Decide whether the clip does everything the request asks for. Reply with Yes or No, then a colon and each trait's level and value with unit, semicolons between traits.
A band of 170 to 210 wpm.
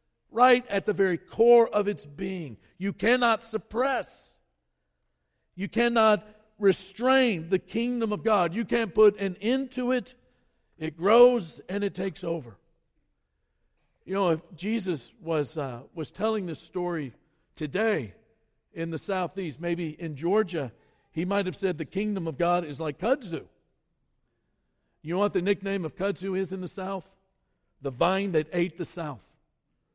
No: average, 150 wpm